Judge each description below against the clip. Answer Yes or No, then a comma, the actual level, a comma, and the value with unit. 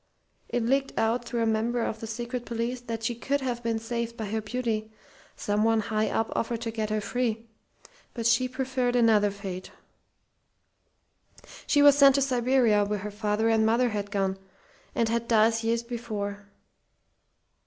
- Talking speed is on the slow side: No, average, 165 wpm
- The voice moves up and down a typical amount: No, narrow, 2.0 semitones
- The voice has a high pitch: Yes, high, 230 Hz